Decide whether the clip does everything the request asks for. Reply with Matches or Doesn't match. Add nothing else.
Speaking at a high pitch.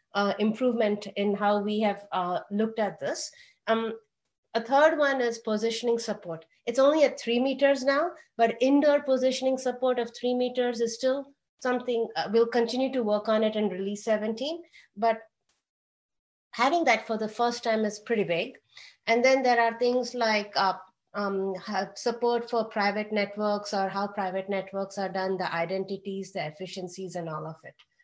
Matches